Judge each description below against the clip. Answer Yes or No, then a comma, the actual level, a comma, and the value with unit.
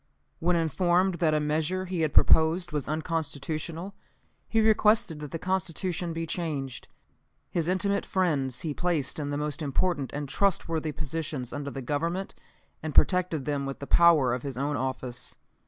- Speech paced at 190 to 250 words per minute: No, average, 160 wpm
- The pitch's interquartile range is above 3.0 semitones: Yes, average, 3.5 semitones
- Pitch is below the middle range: No, medium, 160 Hz